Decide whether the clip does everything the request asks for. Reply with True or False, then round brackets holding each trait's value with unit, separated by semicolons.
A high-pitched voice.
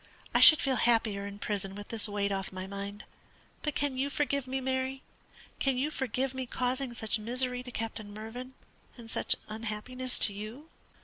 True (240 Hz)